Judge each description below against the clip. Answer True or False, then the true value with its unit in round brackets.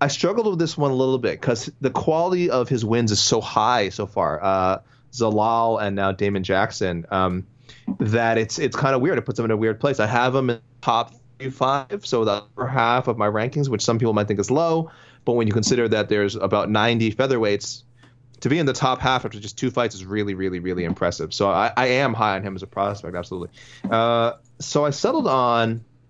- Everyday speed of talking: False (230 wpm)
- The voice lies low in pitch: True (115 Hz)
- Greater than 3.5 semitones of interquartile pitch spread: True (3.9 semitones)